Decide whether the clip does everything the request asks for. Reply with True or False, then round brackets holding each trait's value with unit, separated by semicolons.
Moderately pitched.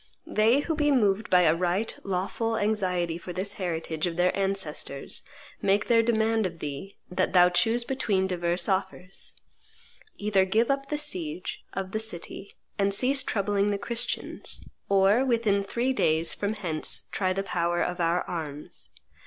False (195 Hz)